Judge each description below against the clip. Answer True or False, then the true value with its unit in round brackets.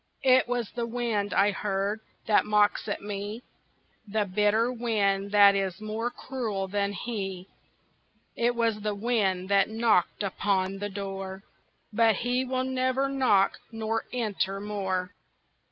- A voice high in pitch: True (210 Hz)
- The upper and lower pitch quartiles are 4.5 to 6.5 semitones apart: False (2.9 semitones)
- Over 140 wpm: False (135 wpm)